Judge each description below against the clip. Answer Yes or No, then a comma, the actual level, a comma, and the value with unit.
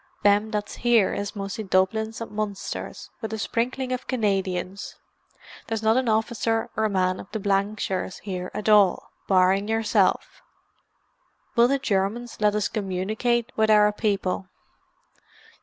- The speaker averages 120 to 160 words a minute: Yes, average, 140 wpm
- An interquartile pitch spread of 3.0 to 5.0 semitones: No, narrow, 2.4 semitones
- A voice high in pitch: Yes, high, 210 Hz